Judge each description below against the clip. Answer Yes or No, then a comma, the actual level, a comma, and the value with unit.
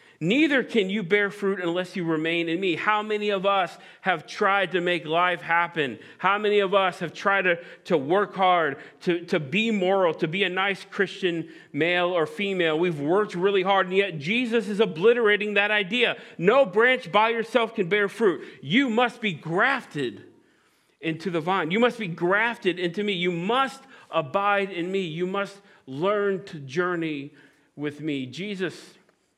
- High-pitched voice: Yes, high, 195 Hz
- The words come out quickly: No, average, 175 wpm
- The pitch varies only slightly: No, average, 3.2 semitones